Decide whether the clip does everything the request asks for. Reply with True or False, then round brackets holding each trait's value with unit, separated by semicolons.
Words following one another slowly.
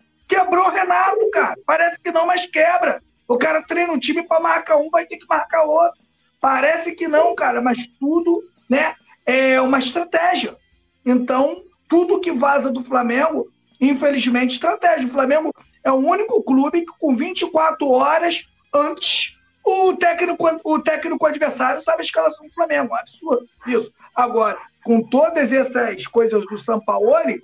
False (155 wpm)